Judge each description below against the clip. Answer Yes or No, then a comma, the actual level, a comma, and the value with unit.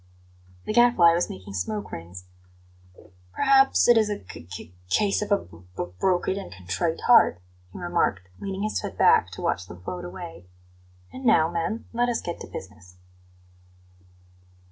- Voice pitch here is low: No, medium, 165 Hz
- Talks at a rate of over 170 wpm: No, average, 165 wpm